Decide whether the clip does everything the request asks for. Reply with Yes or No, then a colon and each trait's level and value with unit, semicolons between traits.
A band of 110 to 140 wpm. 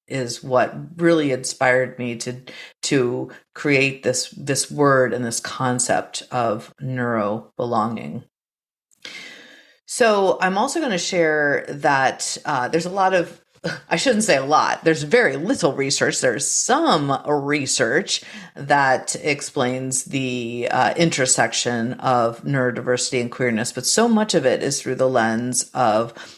Yes: slow, 135 wpm